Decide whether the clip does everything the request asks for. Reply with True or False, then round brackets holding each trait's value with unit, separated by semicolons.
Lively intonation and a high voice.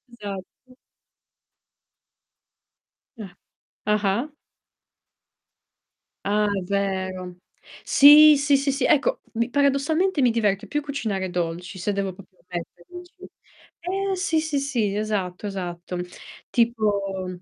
True (6.8 semitones; 210 Hz)